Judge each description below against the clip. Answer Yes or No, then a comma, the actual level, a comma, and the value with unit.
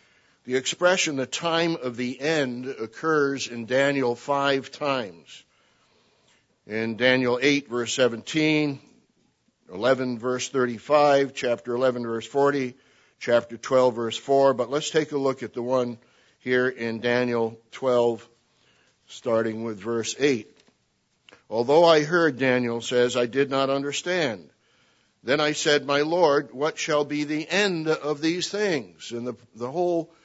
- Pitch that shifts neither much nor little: Yes, average, 3.6 semitones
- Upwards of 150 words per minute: No, average, 140 wpm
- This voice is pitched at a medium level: No, low, 130 Hz